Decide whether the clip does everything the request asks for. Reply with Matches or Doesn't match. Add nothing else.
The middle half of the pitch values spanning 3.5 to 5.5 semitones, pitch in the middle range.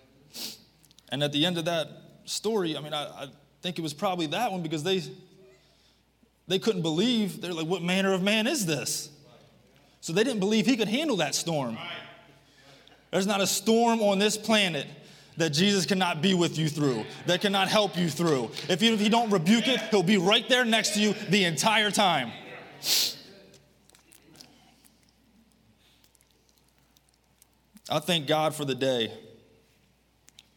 Matches